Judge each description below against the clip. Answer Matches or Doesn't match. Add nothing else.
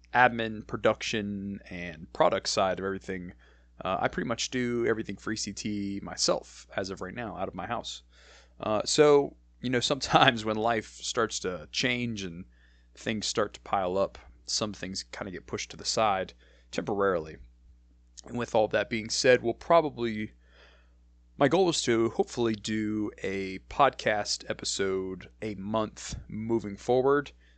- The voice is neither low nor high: Doesn't match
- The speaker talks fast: Doesn't match